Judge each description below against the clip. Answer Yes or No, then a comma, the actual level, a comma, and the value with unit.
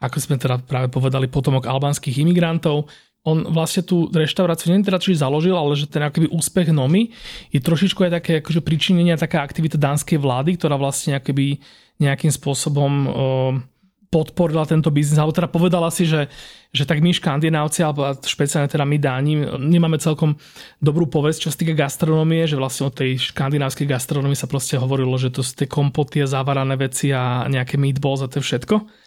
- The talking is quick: Yes, fast, 180 wpm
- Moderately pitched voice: Yes, medium, 150 Hz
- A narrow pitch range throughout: No, average, 3.0 semitones